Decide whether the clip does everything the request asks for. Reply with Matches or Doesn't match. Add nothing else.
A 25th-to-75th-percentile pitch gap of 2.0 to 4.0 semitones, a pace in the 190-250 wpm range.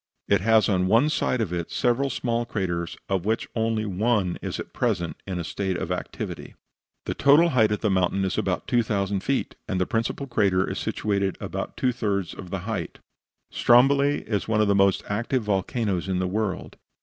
Matches